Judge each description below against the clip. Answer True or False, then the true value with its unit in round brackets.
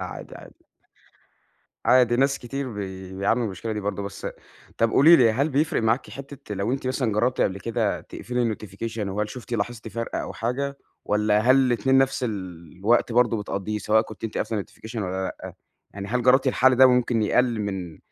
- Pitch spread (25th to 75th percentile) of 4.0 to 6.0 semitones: False (3.6 semitones)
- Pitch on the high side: False (115 Hz)